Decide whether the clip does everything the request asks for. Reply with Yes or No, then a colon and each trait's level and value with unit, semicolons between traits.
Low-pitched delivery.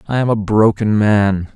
Yes: low, 105 Hz